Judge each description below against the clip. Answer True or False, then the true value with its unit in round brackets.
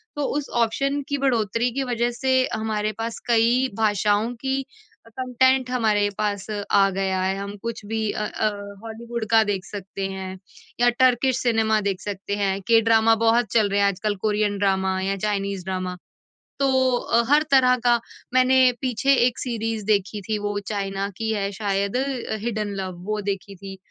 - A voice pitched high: True (220 Hz)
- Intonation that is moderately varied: True (3.3 semitones)